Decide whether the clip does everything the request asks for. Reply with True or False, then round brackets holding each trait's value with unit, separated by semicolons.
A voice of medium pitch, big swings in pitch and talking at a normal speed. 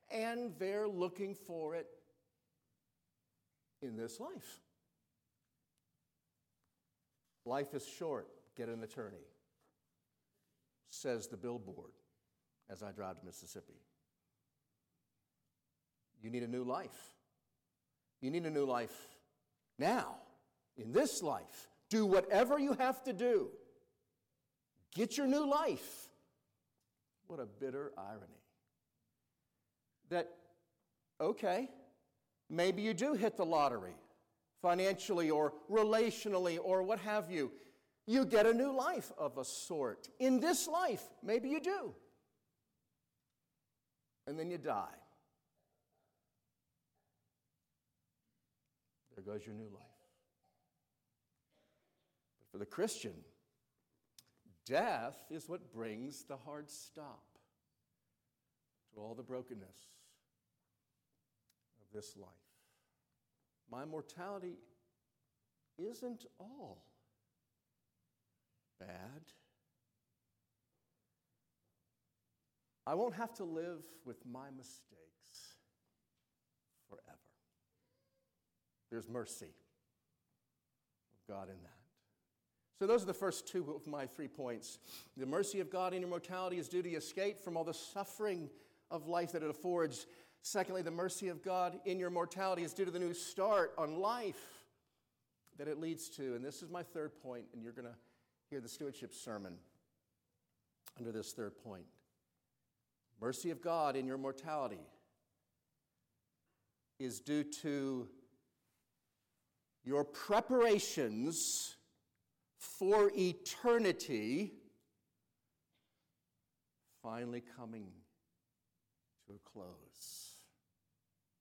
False (160 Hz; 7.9 semitones; 105 wpm)